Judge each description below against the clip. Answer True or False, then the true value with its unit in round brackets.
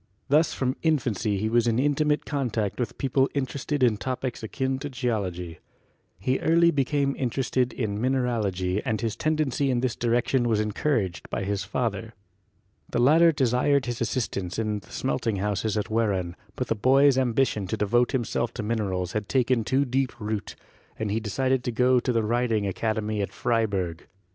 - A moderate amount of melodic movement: True (3.8 semitones)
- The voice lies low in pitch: True (120 Hz)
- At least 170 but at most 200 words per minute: True (175 wpm)